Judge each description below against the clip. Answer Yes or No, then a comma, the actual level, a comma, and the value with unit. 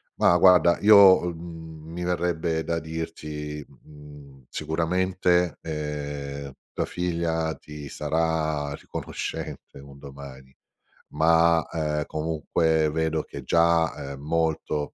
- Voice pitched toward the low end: Yes, very low, 80 Hz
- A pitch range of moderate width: No, narrow, 2.1 semitones